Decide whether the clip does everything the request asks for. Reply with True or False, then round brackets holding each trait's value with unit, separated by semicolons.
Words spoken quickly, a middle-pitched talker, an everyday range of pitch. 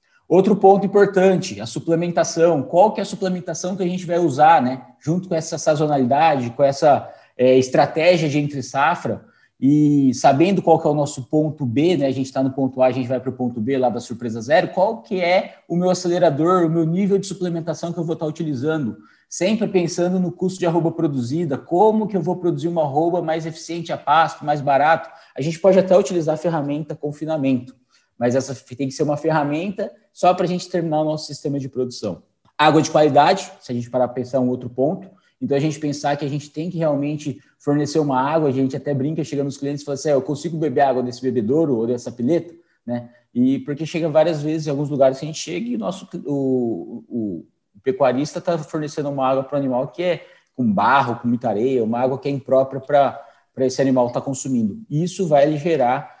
True (225 wpm; 155 Hz; 4.2 semitones)